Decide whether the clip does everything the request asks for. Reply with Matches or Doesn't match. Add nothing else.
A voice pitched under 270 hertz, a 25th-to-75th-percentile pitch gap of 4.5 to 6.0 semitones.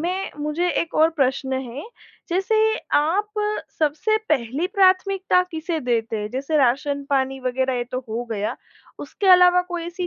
Doesn't match